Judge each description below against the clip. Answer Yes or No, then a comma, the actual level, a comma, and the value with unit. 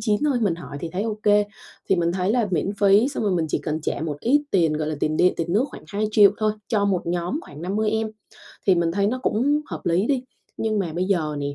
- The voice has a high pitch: Yes, high, 195 Hz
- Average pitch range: Yes, average, 4.2 semitones